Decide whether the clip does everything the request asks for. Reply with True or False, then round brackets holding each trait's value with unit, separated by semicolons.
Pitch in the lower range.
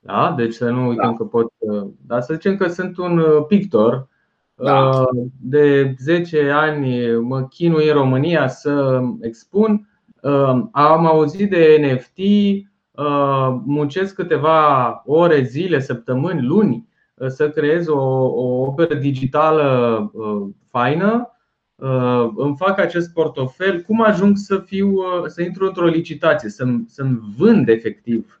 False (150 Hz)